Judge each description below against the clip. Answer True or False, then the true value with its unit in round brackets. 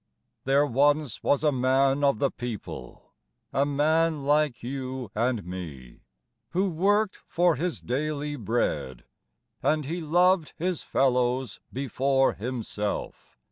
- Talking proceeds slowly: True (120 wpm)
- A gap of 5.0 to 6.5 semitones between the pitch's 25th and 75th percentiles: False (3.8 semitones)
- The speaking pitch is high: False (135 Hz)